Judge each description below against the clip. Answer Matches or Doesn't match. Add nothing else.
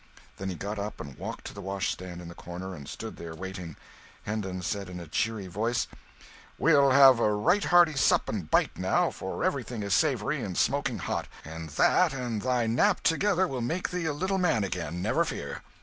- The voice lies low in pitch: Matches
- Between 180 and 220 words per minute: Matches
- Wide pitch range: Matches